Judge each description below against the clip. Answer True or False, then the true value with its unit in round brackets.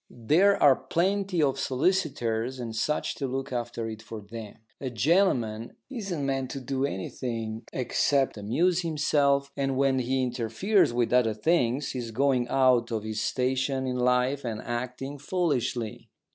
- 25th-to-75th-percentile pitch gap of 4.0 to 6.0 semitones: False (3.2 semitones)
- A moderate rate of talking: True (155 wpm)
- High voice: False (130 Hz)